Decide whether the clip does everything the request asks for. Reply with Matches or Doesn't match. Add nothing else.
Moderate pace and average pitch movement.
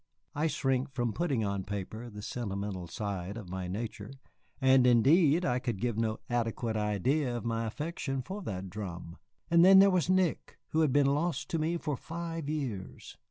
Doesn't match